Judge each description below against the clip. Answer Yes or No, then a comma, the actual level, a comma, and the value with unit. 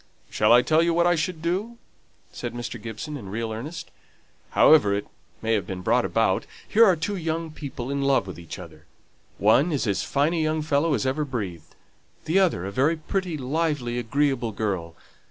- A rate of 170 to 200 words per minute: Yes, average, 190 wpm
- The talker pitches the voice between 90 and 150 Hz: Yes, medium, 140 Hz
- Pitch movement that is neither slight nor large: No, wide, 6.6 semitones